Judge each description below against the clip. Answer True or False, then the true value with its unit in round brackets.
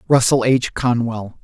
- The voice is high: False (120 Hz)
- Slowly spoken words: True (125 wpm)